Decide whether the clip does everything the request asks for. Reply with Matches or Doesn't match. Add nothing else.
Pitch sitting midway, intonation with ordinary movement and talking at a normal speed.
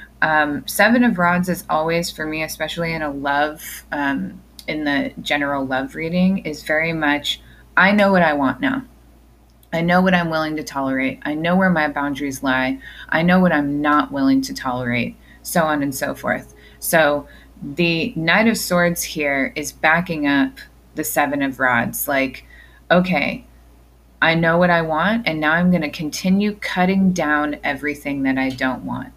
Matches